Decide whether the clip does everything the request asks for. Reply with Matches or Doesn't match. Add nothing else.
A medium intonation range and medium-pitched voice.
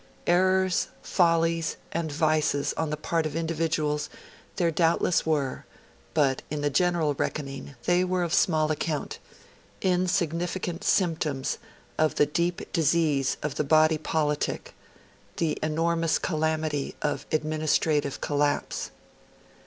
Doesn't match